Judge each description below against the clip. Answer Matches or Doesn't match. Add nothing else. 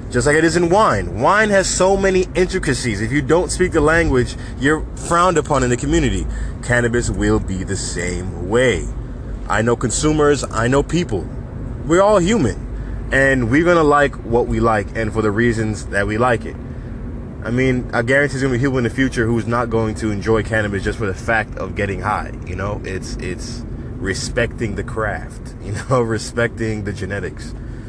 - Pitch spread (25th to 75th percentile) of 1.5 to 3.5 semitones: Doesn't match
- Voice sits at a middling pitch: Doesn't match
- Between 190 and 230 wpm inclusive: Matches